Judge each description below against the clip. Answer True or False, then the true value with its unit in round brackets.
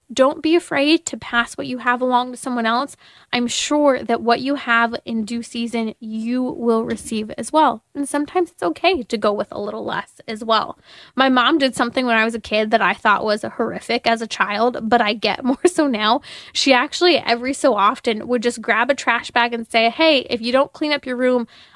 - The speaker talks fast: True (225 wpm)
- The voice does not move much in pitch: False (3.1 semitones)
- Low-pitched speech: False (245 Hz)